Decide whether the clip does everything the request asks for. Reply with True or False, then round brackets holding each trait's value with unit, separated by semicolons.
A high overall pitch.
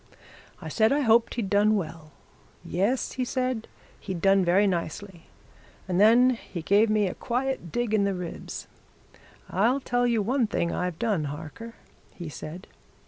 True (205 Hz)